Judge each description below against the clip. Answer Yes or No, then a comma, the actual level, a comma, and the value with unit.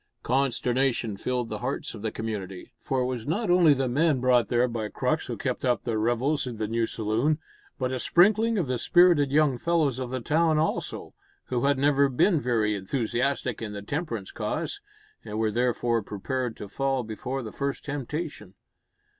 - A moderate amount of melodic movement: Yes, average, 3.8 semitones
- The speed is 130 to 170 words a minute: No, average, 185 wpm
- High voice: No, low, 125 Hz